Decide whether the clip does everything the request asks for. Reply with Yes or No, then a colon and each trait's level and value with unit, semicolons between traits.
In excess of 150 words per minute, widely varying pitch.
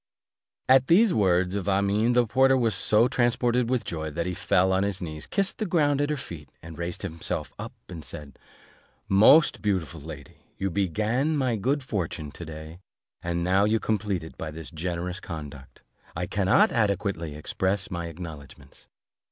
Yes: average, 170 wpm; wide, 6.0 semitones